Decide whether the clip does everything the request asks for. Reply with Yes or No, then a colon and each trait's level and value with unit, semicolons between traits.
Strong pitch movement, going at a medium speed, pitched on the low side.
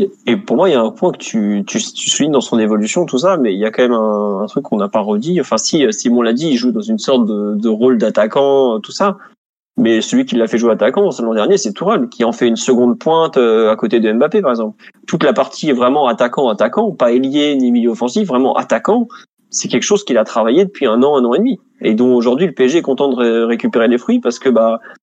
No: wide, 8.9 semitones; fast, 270 wpm; low, 125 Hz